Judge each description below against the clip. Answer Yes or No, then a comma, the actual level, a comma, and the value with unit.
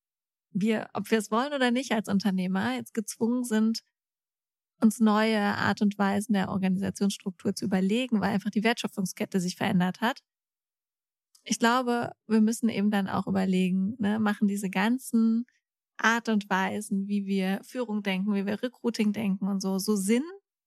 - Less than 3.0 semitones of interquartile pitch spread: Yes, narrow, 2.4 semitones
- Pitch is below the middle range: No, high, 210 Hz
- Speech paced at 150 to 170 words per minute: Yes, average, 160 wpm